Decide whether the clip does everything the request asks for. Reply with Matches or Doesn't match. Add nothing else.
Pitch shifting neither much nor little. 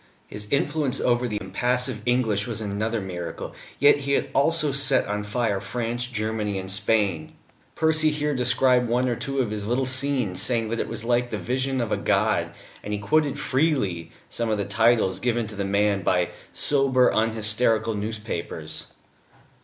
Matches